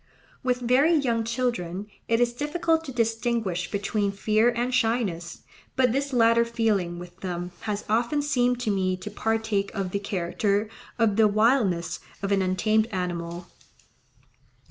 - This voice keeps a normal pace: Yes, average, 145 wpm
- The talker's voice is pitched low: No, high, 220 Hz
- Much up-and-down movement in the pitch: No, average, 4.2 semitones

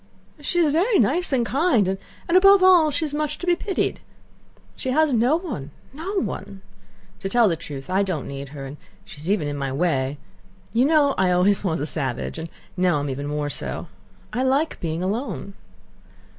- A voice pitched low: No, high, 205 Hz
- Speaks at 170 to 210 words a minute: Yes, average, 185 wpm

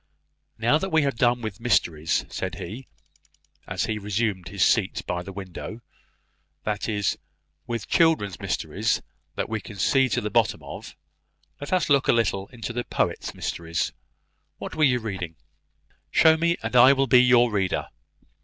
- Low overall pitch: Yes, low, 115 Hz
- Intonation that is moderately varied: Yes, average, 4.8 semitones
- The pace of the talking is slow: No, average, 165 wpm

